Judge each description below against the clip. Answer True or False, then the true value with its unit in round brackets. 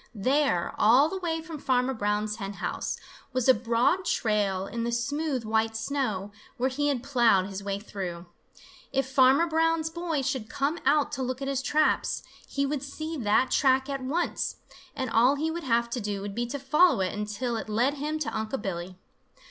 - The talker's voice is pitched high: True (255 Hz)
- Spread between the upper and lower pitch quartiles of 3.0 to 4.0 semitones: False (5.1 semitones)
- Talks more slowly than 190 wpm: False (195 wpm)